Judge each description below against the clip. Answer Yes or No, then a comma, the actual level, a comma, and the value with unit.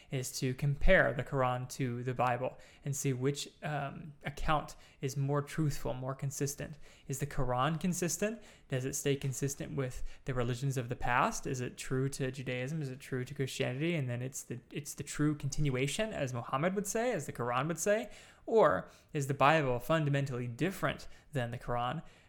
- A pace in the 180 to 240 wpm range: Yes, average, 185 wpm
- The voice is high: No, medium, 140 Hz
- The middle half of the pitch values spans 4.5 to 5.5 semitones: No, narrow, 2.6 semitones